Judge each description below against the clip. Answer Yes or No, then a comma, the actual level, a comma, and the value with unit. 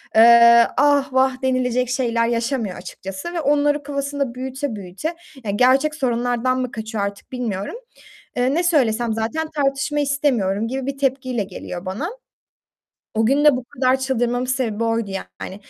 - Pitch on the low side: No, very high, 255 Hz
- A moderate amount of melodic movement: Yes, average, 3.3 semitones